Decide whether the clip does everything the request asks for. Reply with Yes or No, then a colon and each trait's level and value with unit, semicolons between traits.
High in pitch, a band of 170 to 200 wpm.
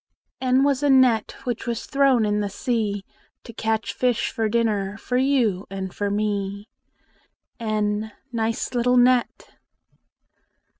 No: high, 225 Hz; slow, 135 wpm